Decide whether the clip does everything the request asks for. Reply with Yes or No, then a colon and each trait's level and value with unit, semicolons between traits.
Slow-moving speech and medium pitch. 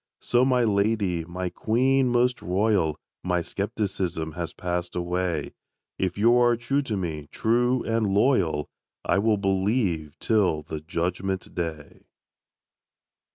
No: slow, 125 wpm; very low, 95 Hz